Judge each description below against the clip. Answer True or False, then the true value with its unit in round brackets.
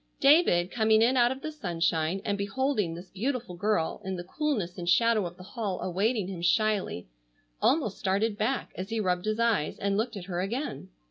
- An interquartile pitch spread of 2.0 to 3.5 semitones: False (4.4 semitones)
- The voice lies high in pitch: True (205 Hz)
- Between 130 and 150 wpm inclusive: False (195 wpm)